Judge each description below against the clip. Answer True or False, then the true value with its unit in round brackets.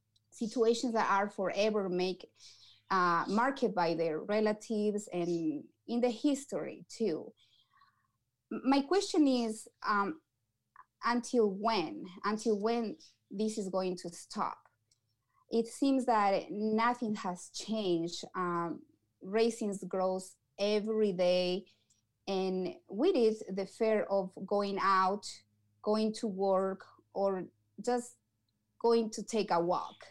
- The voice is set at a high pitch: True (205 Hz)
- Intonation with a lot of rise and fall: False (4.1 semitones)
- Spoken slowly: True (115 wpm)